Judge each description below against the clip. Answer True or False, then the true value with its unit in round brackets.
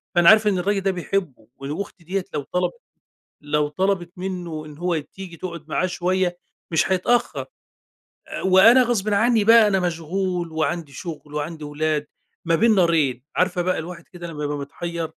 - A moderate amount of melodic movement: True (3.4 semitones)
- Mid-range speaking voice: True (175 Hz)